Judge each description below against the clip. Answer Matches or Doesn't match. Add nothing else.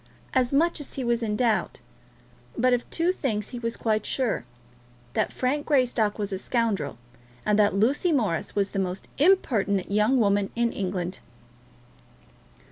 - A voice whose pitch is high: Matches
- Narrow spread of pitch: Doesn't match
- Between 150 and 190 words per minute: Matches